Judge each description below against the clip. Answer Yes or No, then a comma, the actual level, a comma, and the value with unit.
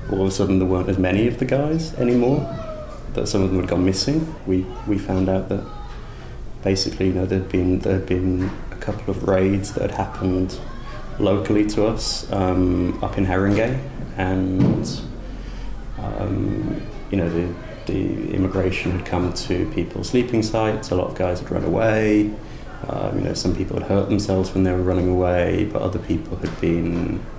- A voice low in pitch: Yes, very low, 95 Hz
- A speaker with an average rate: Yes, average, 180 wpm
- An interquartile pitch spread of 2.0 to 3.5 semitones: Yes, average, 2.9 semitones